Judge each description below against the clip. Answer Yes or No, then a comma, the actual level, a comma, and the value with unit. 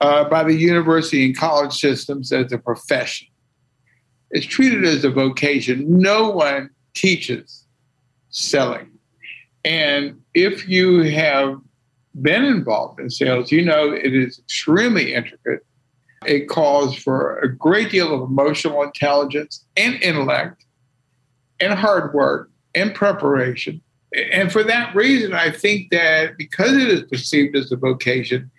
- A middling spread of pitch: Yes, average, 4.8 semitones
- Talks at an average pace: No, slow, 130 wpm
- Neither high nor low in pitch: Yes, medium, 145 Hz